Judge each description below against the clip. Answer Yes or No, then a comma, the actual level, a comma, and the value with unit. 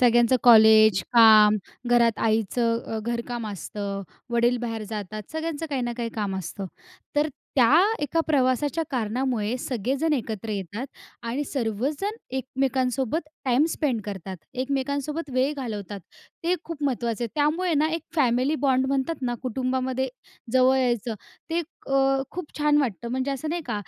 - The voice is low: No, very high, 255 Hz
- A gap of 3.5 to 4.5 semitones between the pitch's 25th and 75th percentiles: Yes, average, 3.8 semitones